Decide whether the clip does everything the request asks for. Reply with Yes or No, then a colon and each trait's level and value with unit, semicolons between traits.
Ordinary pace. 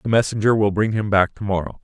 No: fast, 260 wpm